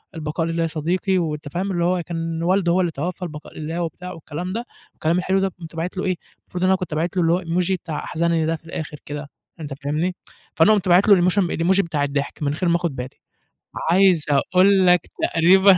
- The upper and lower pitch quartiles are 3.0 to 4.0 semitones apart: No, narrow, 2.5 semitones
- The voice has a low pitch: No, medium, 170 Hz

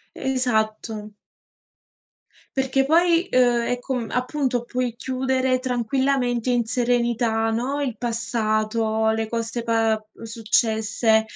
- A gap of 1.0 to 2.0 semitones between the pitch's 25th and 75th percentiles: No, narrow, 2.4 semitones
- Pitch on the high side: Yes, high, 240 Hz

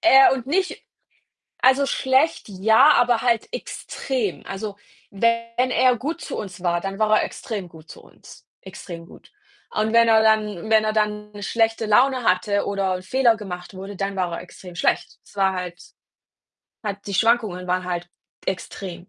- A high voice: Yes, high, 210 Hz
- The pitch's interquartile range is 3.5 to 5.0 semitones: Yes, average, 3.8 semitones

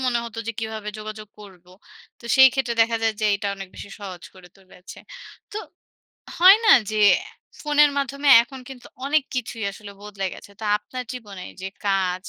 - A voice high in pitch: Yes, high, 220 Hz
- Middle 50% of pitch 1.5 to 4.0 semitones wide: No, average, 4.6 semitones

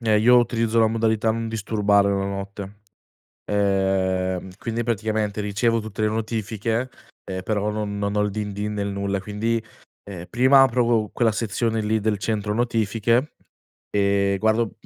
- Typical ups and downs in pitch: No, narrow, 2.1 semitones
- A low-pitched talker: Yes, low, 105 Hz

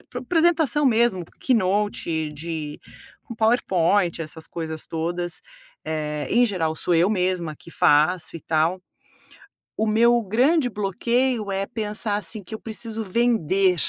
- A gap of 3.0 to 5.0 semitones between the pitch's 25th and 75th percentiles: No, wide, 5.6 semitones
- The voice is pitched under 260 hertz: Yes, high, 195 Hz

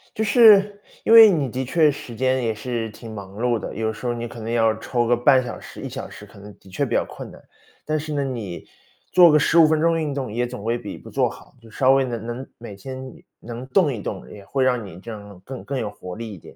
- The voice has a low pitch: Yes, low, 120 Hz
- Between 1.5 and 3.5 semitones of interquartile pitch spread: No, average, 4.2 semitones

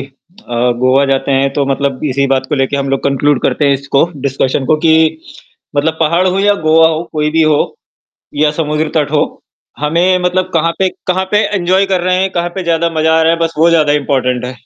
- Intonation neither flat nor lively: Yes, average, 3.5 semitones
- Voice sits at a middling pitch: Yes, medium, 155 Hz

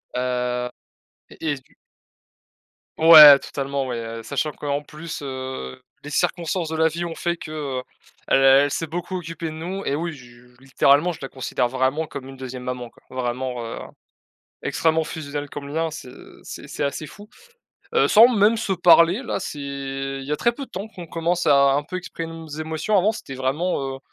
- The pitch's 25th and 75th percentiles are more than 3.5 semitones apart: Yes, average, 3.9 semitones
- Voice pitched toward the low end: No, medium, 145 Hz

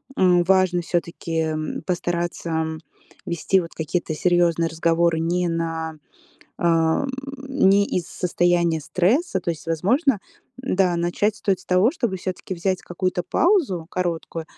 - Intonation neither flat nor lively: No, narrow, 2.1 semitones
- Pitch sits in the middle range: Yes, medium, 175 Hz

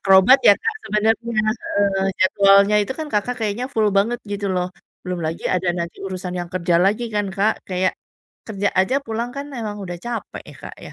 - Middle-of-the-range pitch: No, high, 200 Hz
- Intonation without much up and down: No, average, 3.2 semitones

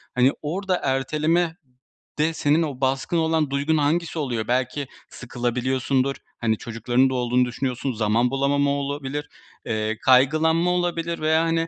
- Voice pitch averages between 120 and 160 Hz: Yes, medium, 140 Hz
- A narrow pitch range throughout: No, average, 4.1 semitones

